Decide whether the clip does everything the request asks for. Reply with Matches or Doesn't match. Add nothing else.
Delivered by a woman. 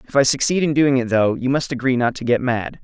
Doesn't match